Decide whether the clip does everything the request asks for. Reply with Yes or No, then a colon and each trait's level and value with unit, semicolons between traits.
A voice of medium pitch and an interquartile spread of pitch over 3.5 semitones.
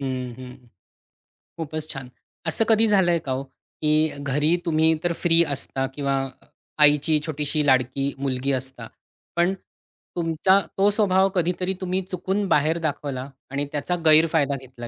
Yes: medium, 155 Hz; average, 4.2 semitones